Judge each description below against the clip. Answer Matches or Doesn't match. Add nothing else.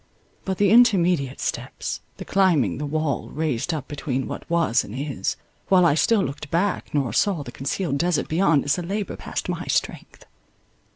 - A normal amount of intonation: Matches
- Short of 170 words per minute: Doesn't match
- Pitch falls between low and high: Matches